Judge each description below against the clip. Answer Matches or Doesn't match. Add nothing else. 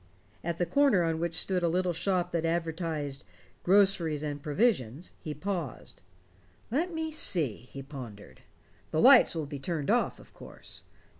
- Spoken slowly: Doesn't match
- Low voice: Doesn't match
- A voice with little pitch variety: Doesn't match